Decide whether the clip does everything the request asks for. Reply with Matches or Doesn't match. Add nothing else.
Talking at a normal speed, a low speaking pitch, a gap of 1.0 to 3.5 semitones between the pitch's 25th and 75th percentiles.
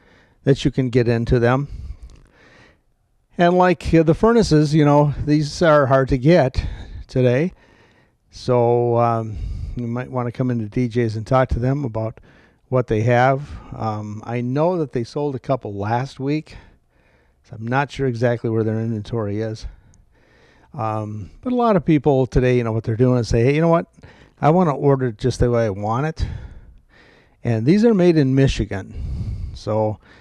Doesn't match